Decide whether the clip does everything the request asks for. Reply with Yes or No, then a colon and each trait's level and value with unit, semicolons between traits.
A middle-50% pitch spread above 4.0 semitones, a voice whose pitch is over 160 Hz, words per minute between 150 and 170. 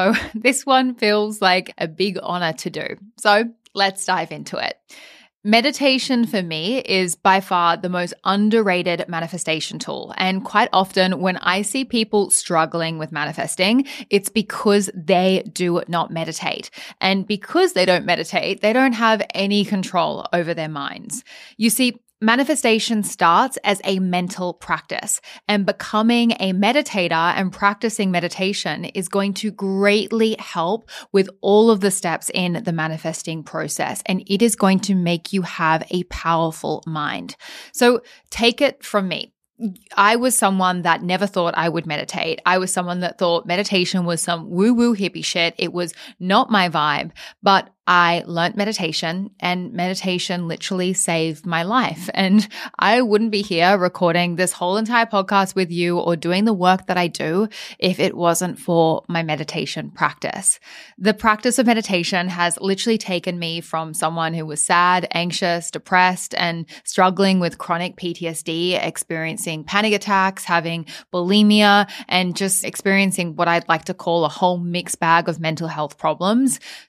No: average, 3.3 semitones; medium, 185 Hz; average, 160 wpm